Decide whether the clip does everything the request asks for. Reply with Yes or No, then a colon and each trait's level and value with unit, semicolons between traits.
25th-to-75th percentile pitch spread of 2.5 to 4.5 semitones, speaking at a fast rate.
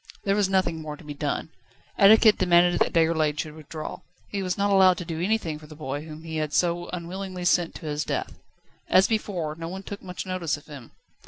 Yes: average, 3.5 semitones; fast, 220 wpm